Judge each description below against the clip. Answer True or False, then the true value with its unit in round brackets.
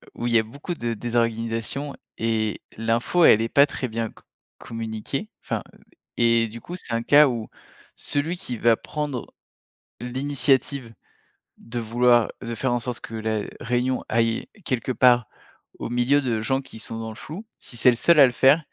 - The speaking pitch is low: True (120 Hz)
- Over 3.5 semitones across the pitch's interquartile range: False (2.9 semitones)